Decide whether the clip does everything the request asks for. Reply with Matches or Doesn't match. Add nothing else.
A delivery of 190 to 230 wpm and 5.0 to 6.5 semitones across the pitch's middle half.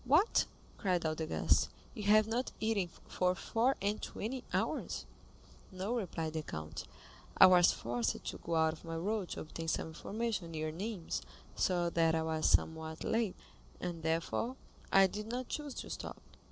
Doesn't match